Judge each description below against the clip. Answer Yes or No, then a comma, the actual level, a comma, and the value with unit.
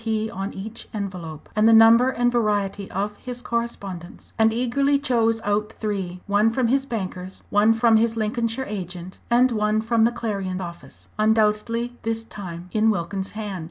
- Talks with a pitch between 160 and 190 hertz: No, high, 220 Hz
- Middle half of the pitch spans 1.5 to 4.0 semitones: Yes, average, 2.8 semitones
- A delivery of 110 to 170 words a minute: Yes, average, 165 wpm